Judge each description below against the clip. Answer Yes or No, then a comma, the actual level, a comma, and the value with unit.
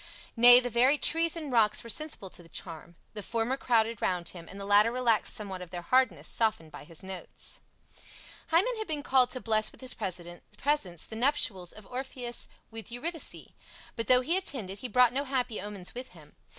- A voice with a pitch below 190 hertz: No, high, 230 Hz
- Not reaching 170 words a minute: No, average, 195 wpm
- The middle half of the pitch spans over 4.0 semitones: Yes, average, 5.2 semitones